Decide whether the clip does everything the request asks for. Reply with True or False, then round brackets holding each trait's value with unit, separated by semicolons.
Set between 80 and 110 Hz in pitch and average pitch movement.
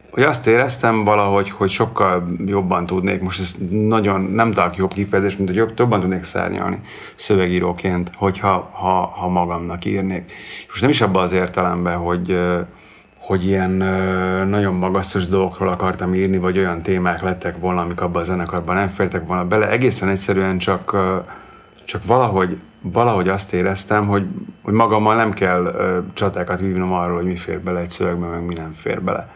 False (95 Hz; 1.6 semitones)